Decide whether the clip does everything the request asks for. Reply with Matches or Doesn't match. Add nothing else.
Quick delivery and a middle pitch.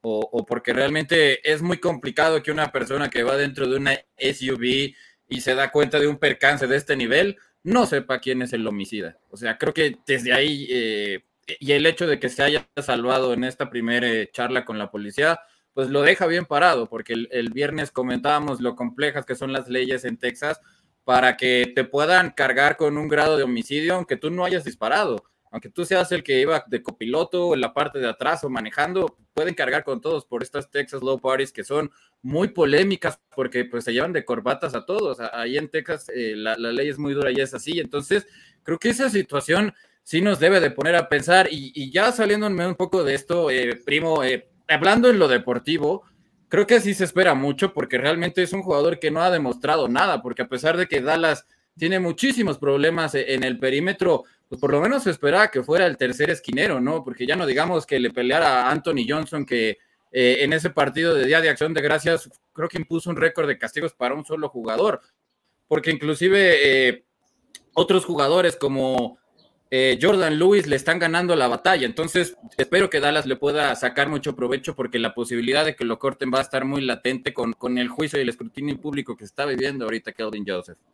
Matches